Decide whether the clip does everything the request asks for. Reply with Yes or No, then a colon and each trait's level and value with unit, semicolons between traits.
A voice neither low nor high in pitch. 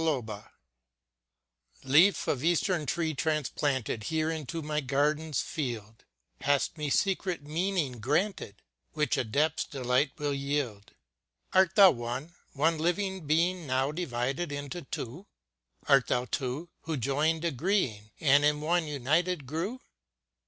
Yes: medium, 150 Hz